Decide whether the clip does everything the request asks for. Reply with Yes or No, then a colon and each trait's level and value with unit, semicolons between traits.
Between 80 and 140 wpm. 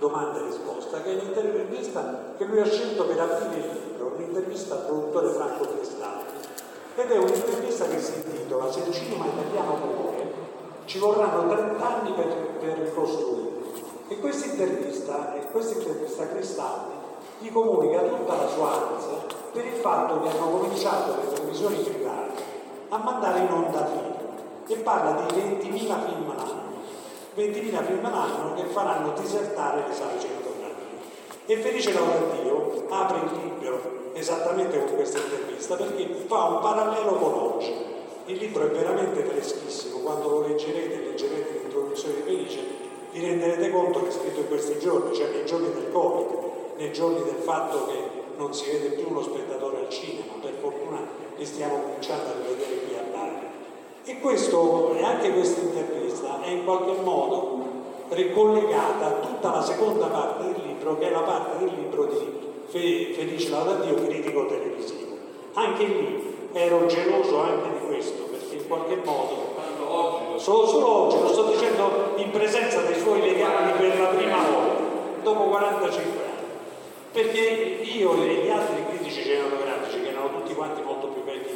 No: average, 155 wpm